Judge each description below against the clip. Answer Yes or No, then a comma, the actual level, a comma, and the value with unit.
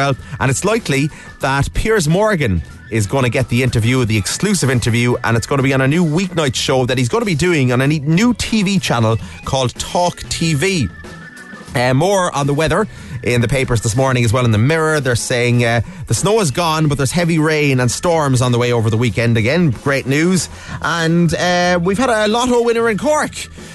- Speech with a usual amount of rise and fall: No, wide, 6.3 semitones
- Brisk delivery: Yes, fast, 215 wpm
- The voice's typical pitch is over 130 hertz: Yes, medium, 140 Hz